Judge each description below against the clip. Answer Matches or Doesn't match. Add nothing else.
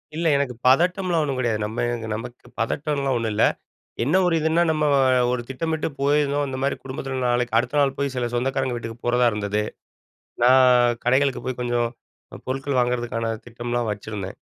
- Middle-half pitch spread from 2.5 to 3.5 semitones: Matches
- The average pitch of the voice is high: Doesn't match